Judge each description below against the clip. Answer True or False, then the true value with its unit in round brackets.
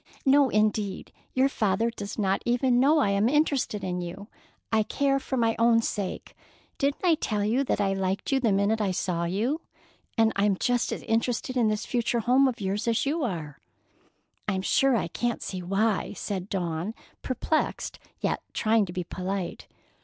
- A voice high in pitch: True (215 Hz)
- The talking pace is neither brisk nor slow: True (180 wpm)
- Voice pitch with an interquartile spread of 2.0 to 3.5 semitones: False (4.2 semitones)